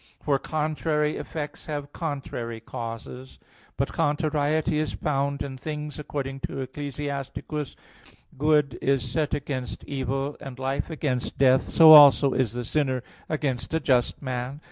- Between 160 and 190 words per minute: No, average, 140 wpm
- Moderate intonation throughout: No, narrow, 2.3 semitones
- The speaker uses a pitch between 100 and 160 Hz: Yes, medium, 140 Hz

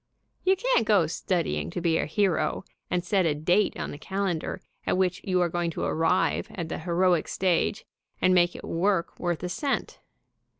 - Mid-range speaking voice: Yes, medium, 180 Hz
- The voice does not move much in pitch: Yes, narrow, 2.2 semitones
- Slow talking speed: No, average, 195 wpm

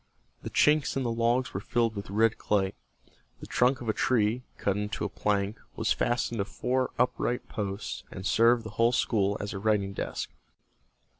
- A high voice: No, low, 110 Hz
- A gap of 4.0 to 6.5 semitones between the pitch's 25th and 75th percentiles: No, average, 3.1 semitones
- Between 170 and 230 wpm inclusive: Yes, average, 180 wpm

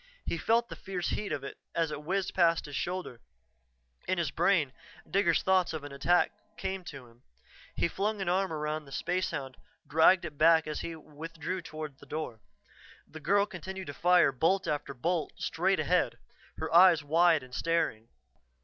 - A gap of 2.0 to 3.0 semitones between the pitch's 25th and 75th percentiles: No, average, 3.8 semitones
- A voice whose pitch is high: No, medium, 165 Hz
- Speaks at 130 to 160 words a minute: No, average, 175 wpm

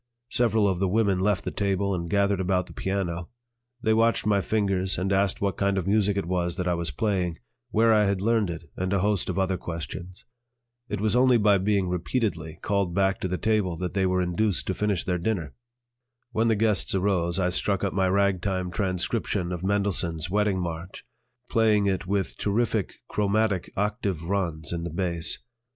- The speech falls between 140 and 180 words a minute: No, average, 190 wpm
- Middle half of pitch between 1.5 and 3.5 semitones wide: Yes, narrow, 2.4 semitones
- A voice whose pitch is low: Yes, very low, 95 Hz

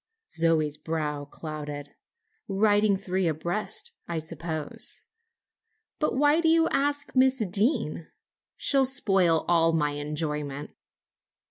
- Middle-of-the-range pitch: Yes, medium, 170 Hz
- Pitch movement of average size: No, wide, 6.3 semitones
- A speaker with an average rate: No, slow, 105 wpm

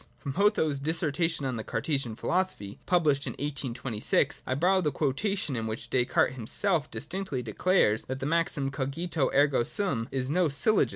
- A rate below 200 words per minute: Yes, average, 160 wpm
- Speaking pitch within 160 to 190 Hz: No, medium, 140 Hz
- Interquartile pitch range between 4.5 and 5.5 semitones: Yes, average, 4.9 semitones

